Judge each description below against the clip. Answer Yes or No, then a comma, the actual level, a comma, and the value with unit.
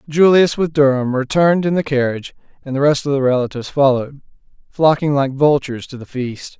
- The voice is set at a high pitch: No, medium, 140 Hz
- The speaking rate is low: No, average, 180 wpm